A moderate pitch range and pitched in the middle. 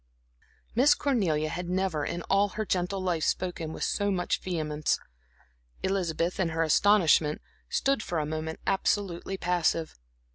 Yes: average, 3.4 semitones; medium, 180 Hz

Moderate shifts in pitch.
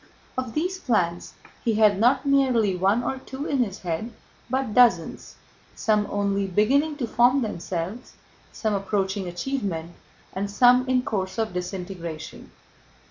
Yes: average, 5.0 semitones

